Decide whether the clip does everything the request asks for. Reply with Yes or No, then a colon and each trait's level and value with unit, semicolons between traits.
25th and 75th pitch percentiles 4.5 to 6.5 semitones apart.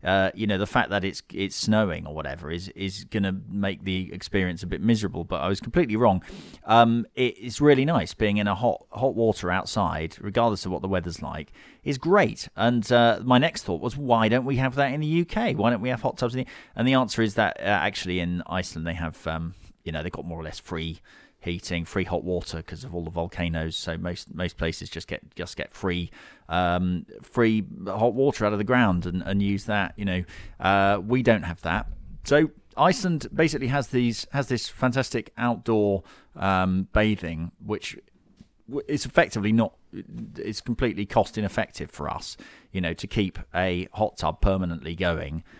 Yes: average, 5.1 semitones